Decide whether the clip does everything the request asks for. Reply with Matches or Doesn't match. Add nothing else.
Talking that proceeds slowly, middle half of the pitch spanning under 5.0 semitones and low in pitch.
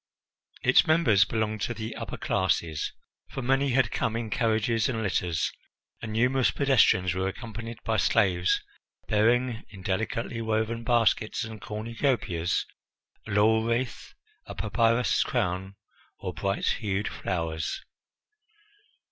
Matches